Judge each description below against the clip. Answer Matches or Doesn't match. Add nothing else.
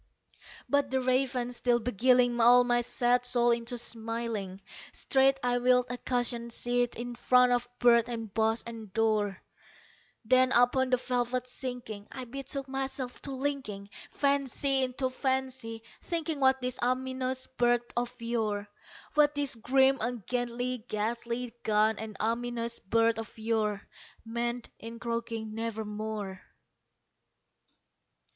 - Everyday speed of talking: Doesn't match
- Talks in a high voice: Matches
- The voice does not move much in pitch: Matches